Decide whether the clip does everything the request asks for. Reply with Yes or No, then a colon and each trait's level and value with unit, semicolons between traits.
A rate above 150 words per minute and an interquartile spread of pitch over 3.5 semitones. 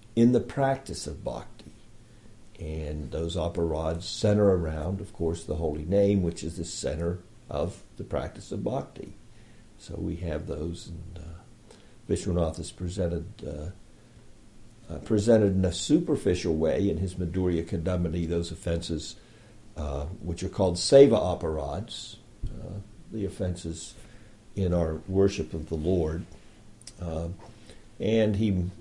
No: slow, 135 wpm; average, 4.5 semitones